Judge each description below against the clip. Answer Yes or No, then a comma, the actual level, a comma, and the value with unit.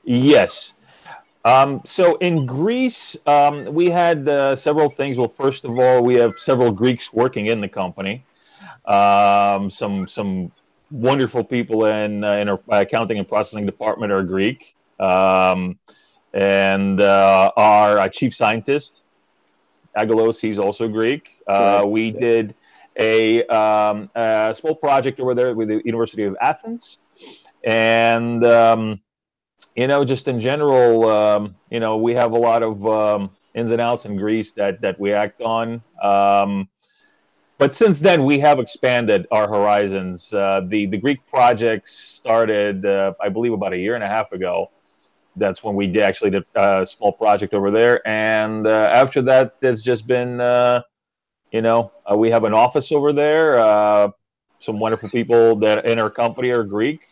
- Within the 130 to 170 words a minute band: Yes, average, 160 wpm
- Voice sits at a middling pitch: No, low, 115 Hz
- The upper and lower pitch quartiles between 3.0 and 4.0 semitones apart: Yes, average, 3.3 semitones